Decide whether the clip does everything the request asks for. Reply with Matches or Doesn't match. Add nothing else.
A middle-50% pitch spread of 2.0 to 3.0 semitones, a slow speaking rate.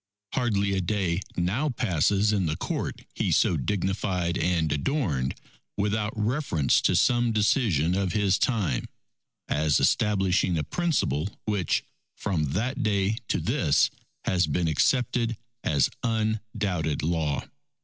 Doesn't match